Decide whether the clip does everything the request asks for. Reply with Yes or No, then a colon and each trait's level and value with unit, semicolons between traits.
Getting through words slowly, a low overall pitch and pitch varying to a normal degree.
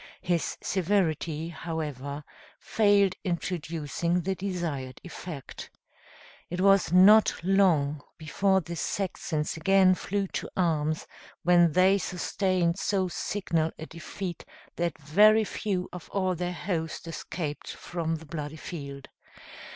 No: slow, 120 wpm; medium, 175 Hz; average, 3.3 semitones